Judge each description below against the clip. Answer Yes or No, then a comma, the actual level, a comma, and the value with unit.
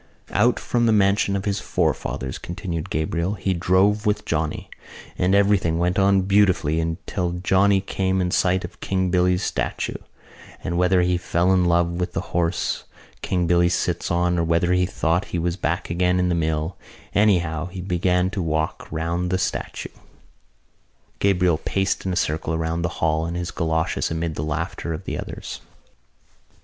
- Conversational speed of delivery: Yes, average, 170 wpm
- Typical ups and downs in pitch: No, narrow, 2.1 semitones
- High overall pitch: No, very low, 90 Hz